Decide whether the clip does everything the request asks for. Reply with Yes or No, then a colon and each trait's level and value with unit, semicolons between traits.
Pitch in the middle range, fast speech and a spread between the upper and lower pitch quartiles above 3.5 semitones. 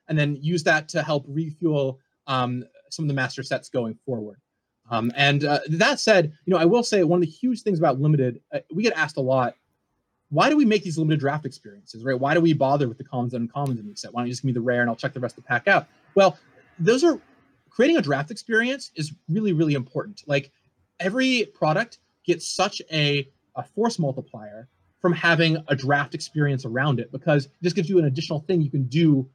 Yes: medium, 145 Hz; fast, 230 wpm; average, 5.0 semitones